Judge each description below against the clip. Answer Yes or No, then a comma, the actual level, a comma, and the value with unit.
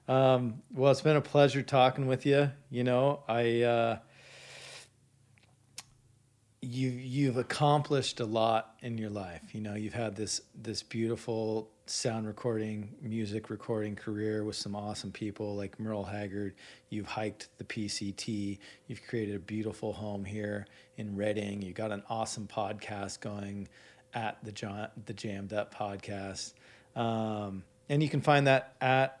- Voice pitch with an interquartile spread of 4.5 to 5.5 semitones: No, average, 3.2 semitones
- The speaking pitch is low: Yes, low, 110 Hz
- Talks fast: No, average, 145 wpm